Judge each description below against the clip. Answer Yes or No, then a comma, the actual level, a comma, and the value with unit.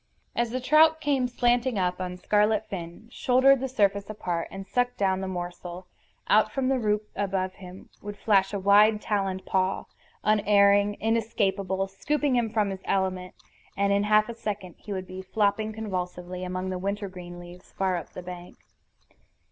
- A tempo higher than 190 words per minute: No, average, 170 wpm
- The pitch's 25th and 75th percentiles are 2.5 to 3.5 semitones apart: Yes, average, 2.8 semitones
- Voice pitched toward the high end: Yes, high, 200 Hz